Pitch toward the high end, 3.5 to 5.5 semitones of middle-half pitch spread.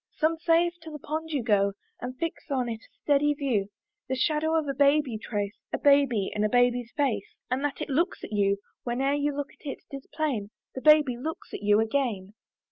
Yes: very high, 275 Hz; average, 5.0 semitones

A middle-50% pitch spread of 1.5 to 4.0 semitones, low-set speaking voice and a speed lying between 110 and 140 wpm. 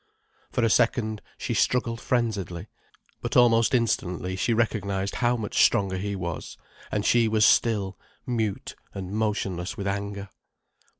Yes: average, 3.1 semitones; low, 105 Hz; slow, 135 wpm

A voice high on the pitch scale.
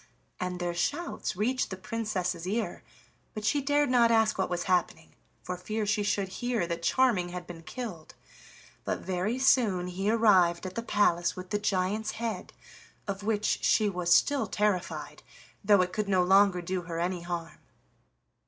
Yes: high, 195 Hz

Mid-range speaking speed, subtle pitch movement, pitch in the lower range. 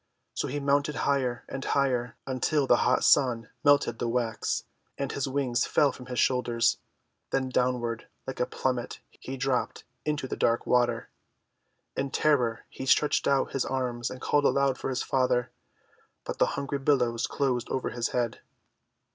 Yes: average, 165 wpm; narrow, 2.2 semitones; low, 130 Hz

